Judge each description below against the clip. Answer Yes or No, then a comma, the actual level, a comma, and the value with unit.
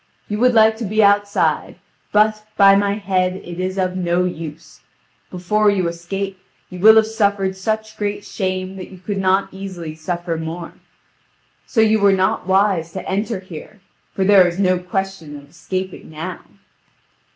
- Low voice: No, high, 190 Hz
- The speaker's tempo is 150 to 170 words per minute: Yes, average, 165 wpm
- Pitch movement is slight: Yes, narrow, 2.3 semitones